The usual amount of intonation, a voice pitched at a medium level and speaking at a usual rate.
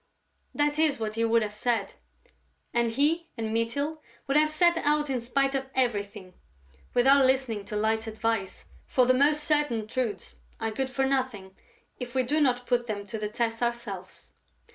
No: average, 3.9 semitones; high, 245 Hz; average, 175 wpm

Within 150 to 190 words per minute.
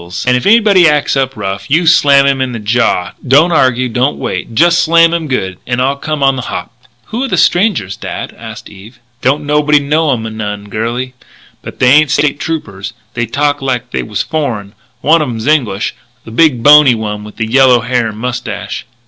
No: average, 200 wpm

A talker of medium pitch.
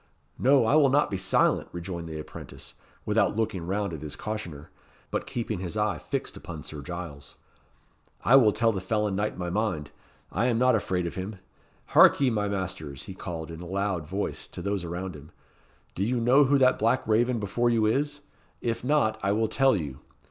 No: low, 100 Hz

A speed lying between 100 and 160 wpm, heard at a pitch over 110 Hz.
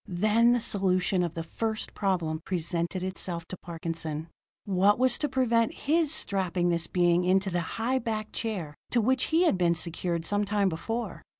No: average, 175 wpm; high, 190 Hz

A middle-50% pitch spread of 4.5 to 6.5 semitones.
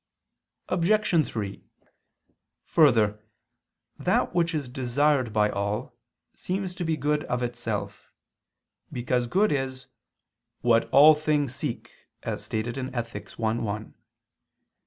Yes: average, 4.9 semitones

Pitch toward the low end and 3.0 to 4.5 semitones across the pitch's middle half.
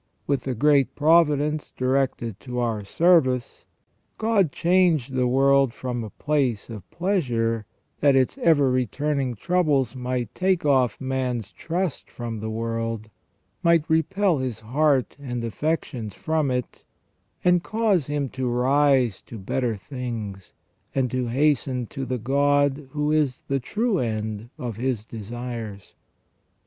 Yes: low, 130 Hz; average, 4.1 semitones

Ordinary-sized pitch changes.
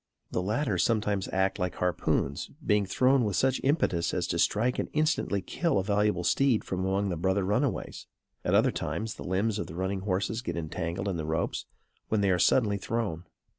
Yes: average, 3.5 semitones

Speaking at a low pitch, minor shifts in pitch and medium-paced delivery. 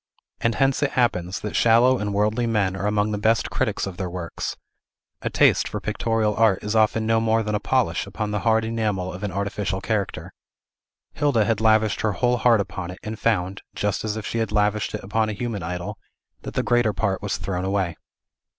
No: low, 105 Hz; narrow, 2.3 semitones; fast, 210 wpm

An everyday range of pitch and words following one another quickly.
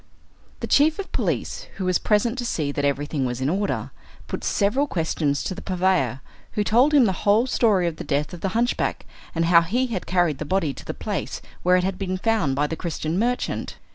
No: wide, 5.9 semitones; fast, 220 wpm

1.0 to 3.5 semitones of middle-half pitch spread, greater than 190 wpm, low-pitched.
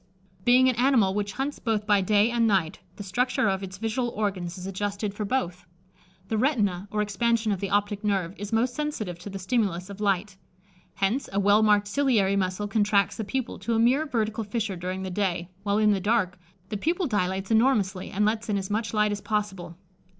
No: average, 2.7 semitones; fast, 205 wpm; high, 205 Hz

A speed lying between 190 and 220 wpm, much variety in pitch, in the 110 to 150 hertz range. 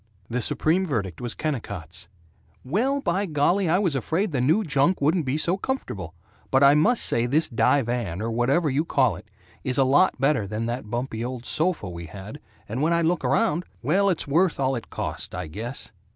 Yes: average, 195 wpm; wide, 6.3 semitones; low, 135 Hz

